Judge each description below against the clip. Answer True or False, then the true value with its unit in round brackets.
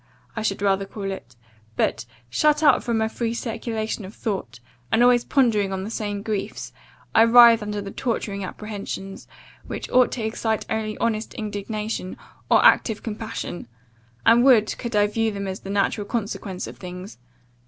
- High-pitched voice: True (215 Hz)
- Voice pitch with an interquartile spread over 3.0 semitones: False (2.4 semitones)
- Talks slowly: False (165 wpm)